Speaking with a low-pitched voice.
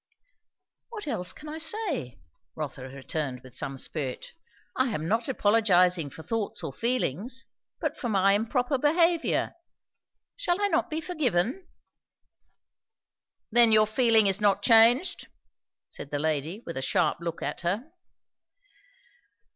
No: high, 220 Hz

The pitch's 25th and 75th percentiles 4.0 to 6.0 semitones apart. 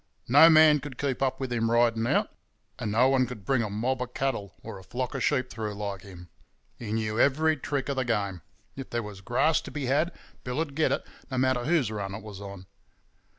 Yes: average, 4.3 semitones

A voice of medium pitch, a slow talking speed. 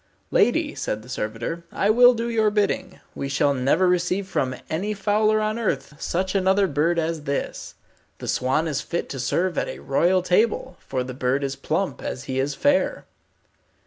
No: medium, 170 Hz; average, 180 wpm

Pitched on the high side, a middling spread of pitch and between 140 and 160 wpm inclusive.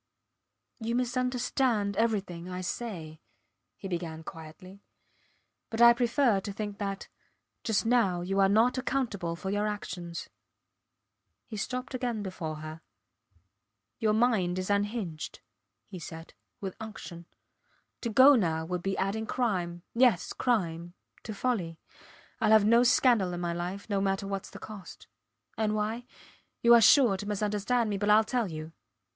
Yes: high, 205 Hz; average, 4.5 semitones; average, 145 wpm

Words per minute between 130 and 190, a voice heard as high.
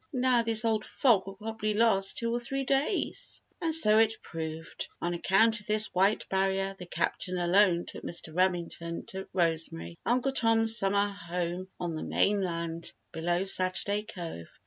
Yes: average, 160 wpm; high, 195 Hz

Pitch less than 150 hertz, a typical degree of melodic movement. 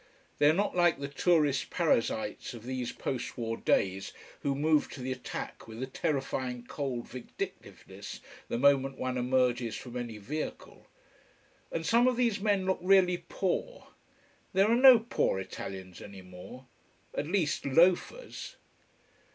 No: low, 135 Hz; wide, 6.6 semitones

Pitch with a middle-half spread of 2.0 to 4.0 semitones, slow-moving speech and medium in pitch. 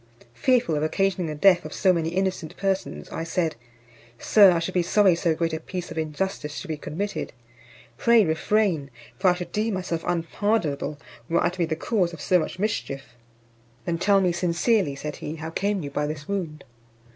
No: average, 3.5 semitones; average, 195 wpm; medium, 175 Hz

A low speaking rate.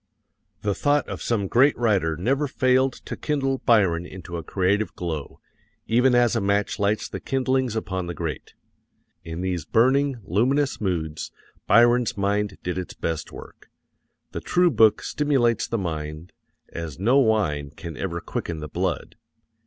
No: average, 155 wpm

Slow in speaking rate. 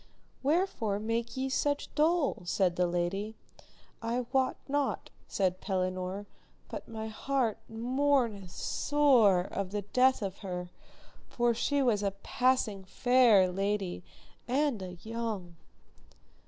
Yes: slow, 120 wpm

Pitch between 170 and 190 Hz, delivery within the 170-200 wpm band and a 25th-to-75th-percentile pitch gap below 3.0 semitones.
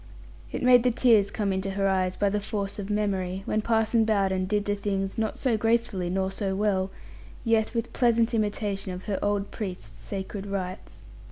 No: high, 200 Hz; average, 185 wpm; narrow, 2.4 semitones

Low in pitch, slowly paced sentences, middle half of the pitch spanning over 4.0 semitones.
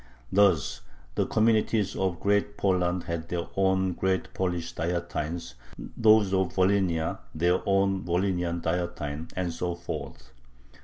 No: very low, 90 Hz; slow, 120 wpm; narrow, 2.4 semitones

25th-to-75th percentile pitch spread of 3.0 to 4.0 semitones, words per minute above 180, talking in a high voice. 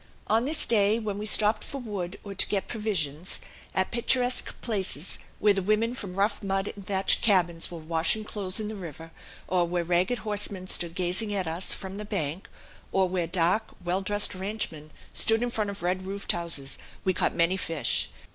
Yes: average, 3.3 semitones; average, 190 wpm; high, 195 Hz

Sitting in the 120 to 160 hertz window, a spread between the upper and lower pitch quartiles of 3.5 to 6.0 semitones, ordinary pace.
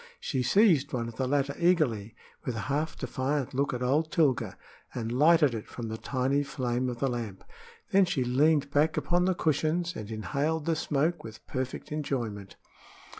Yes: medium, 140 Hz; average, 4.3 semitones; average, 175 wpm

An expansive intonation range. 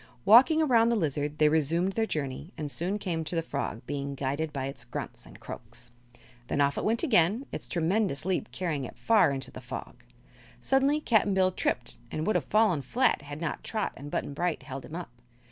Yes: wide, 7.0 semitones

